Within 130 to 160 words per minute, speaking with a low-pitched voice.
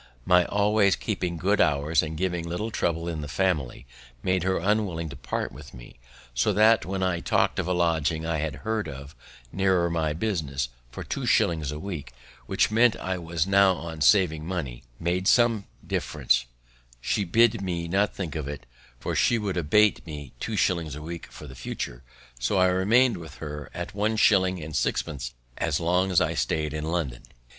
No: average, 190 wpm; very low, 85 Hz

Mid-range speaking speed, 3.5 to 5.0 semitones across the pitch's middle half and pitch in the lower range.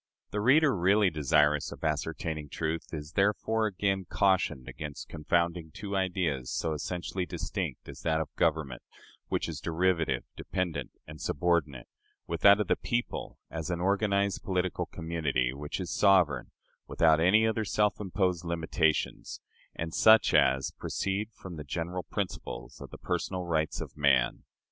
Yes: average, 150 wpm; average, 4.1 semitones; very low, 85 Hz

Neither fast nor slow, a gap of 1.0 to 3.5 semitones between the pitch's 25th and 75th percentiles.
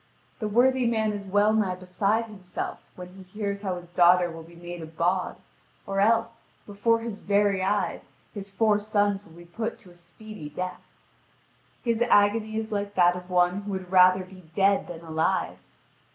Yes: average, 180 wpm; average, 3.0 semitones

